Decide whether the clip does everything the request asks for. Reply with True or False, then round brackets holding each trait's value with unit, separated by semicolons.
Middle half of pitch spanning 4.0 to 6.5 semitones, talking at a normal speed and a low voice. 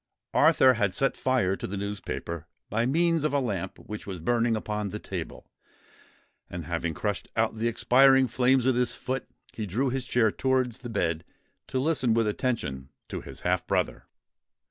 True (4.4 semitones; 175 wpm; 115 Hz)